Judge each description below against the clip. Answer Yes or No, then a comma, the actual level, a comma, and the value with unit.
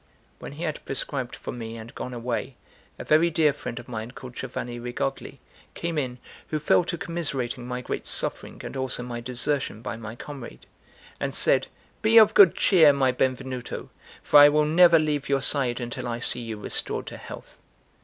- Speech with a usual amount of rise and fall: Yes, average, 3.8 semitones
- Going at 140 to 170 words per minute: No, average, 185 wpm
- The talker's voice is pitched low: Yes, low, 130 Hz